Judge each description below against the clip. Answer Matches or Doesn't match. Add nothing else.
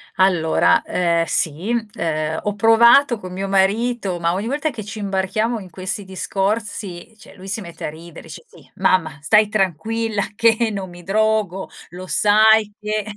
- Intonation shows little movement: Doesn't match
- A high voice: Matches